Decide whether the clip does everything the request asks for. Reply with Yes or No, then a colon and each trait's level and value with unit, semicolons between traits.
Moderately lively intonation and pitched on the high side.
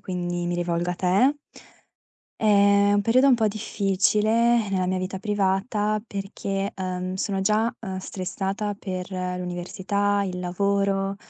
No: narrow, 2.1 semitones; high, 195 Hz